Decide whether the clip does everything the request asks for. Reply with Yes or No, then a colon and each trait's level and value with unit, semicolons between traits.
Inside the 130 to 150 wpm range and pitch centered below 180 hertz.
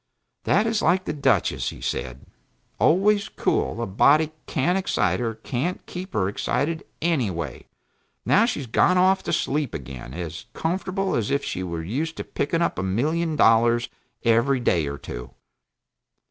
No: average, 160 wpm; low, 135 Hz